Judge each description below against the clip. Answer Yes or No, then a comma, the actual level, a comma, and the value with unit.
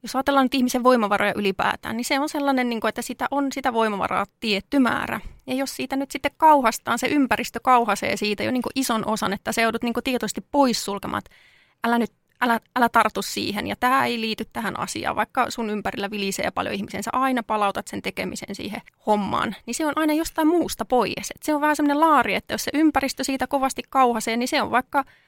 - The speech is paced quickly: Yes, fast, 200 wpm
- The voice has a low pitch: No, high, 245 Hz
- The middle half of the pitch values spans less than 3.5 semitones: No, average, 3.8 semitones